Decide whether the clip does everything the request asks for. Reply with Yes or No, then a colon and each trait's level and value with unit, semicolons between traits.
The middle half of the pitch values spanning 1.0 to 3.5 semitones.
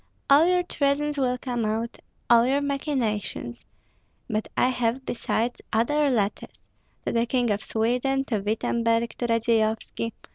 Yes: average, 3.2 semitones